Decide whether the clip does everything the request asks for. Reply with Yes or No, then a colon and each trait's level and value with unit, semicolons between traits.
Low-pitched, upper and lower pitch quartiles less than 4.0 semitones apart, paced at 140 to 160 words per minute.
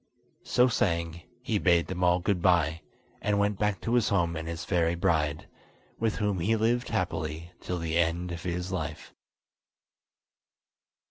Yes: very low, 90 Hz; average, 3.4 semitones; average, 150 wpm